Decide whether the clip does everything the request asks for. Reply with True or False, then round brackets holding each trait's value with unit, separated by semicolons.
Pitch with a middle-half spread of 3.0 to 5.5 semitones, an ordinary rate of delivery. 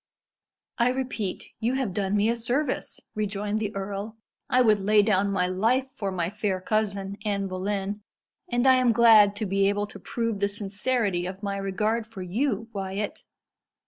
False (2.6 semitones; 175 wpm)